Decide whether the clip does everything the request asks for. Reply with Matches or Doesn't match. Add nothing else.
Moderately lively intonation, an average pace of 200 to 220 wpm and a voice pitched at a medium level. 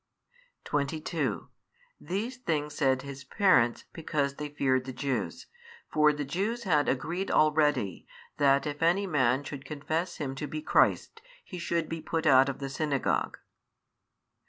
Doesn't match